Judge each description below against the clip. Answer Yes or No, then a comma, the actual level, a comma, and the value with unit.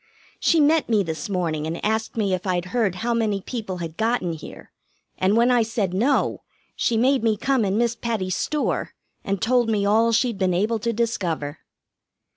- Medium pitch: No, high, 215 Hz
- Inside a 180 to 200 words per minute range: Yes, average, 190 wpm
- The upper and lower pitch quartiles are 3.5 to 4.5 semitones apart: Yes, average, 4.1 semitones